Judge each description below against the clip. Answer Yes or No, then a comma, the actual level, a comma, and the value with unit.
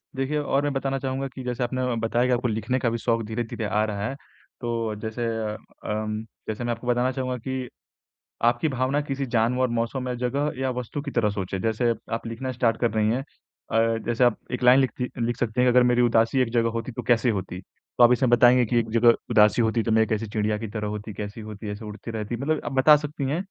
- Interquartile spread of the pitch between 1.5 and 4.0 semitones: Yes, narrow, 2.4 semitones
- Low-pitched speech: Yes, low, 120 Hz